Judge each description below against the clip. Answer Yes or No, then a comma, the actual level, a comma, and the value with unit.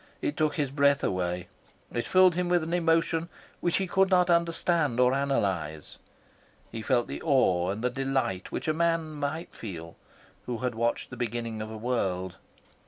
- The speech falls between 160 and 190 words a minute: Yes, average, 170 wpm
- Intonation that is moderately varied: No, wide, 7.1 semitones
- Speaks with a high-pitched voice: No, low, 135 Hz